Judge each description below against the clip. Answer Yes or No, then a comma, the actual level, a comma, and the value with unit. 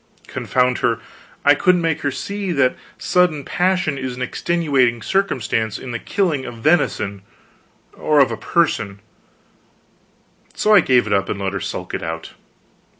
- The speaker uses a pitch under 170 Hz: Yes, low, 135 Hz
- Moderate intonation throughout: No, wide, 7.0 semitones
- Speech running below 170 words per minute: Yes, average, 155 wpm